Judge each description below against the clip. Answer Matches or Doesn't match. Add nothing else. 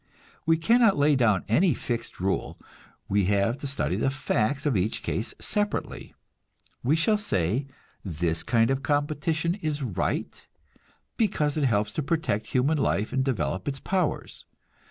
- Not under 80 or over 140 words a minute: Doesn't match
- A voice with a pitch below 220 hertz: Matches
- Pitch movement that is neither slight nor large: Doesn't match